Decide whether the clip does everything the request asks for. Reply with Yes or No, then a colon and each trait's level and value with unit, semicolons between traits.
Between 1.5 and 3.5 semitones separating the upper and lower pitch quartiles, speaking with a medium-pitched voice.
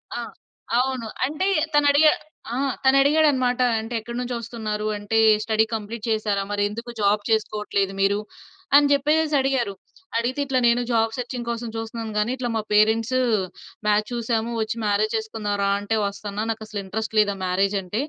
No: average, 3.1 semitones; high, 225 Hz